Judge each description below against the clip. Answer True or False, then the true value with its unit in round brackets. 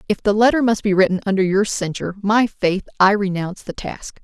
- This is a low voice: False (200 Hz)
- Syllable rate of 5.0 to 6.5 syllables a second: True (5.8 syllables/s)